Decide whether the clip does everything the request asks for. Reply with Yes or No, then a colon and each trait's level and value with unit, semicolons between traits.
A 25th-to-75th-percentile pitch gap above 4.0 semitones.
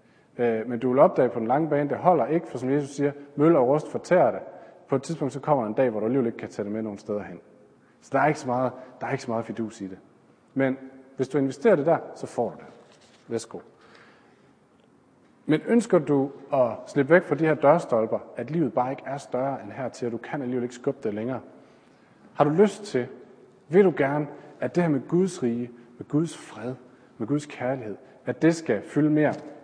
No: average, 3.2 semitones